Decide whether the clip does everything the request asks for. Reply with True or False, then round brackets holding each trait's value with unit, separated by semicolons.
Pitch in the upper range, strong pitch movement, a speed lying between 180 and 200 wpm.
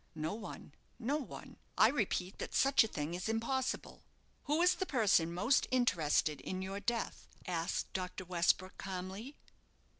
False (195 Hz; 5.7 semitones; 150 wpm)